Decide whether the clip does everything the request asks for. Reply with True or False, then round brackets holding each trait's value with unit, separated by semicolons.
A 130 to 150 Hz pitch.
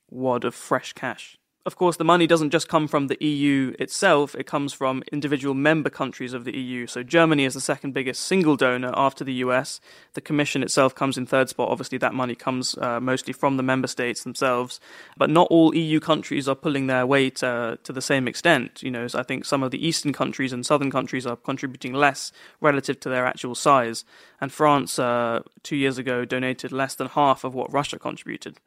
True (135 Hz)